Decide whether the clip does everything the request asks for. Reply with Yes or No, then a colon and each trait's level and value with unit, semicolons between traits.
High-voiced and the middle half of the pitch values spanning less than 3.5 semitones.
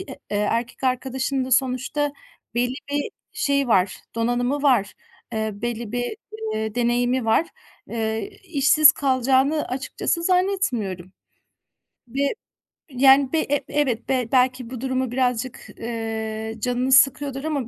Yes: very high, 255 Hz; average, 3.0 semitones